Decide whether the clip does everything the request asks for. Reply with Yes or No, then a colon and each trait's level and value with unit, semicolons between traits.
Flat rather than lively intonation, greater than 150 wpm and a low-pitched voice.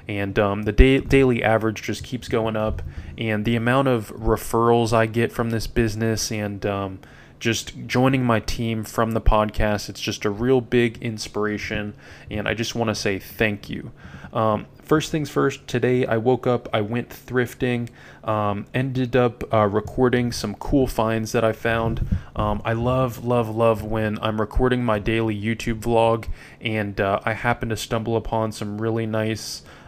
Yes: narrow, 2.1 semitones; average, 175 wpm; low, 115 Hz